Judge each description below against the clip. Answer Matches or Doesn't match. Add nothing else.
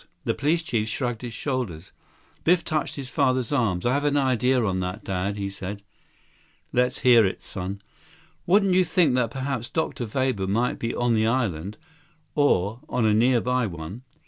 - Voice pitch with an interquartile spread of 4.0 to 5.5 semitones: Matches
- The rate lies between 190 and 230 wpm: Doesn't match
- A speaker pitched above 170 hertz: Doesn't match